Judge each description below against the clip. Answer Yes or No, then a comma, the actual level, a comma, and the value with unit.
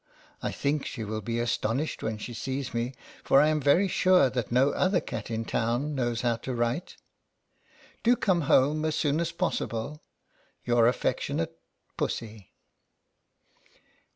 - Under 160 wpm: Yes, average, 150 wpm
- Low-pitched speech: Yes, low, 130 Hz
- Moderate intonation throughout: Yes, average, 4.7 semitones